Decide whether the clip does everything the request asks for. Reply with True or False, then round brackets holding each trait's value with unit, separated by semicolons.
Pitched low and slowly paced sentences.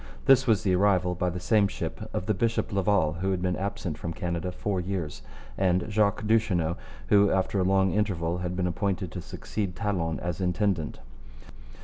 False (95 Hz; 180 wpm)